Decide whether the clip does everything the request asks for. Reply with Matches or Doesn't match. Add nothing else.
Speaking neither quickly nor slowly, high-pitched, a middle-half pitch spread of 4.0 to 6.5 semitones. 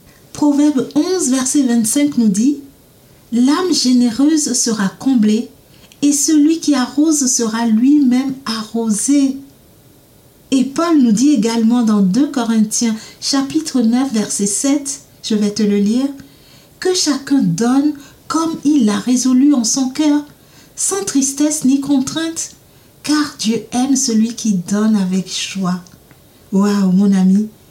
Doesn't match